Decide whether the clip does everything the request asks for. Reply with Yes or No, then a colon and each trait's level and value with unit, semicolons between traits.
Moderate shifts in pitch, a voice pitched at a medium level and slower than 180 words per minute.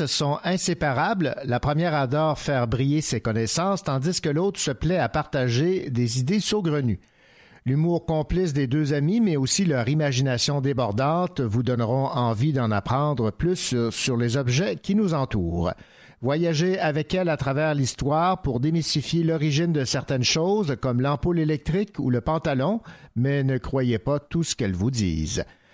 Yes: average, 4.4 semitones; medium, 145 Hz; average, 160 wpm